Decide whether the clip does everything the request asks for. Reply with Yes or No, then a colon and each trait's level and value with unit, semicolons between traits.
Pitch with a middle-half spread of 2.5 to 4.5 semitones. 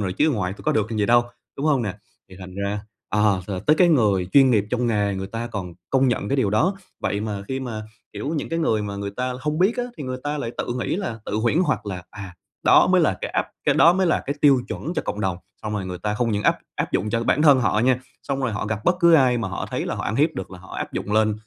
No: average, 5.2 semitones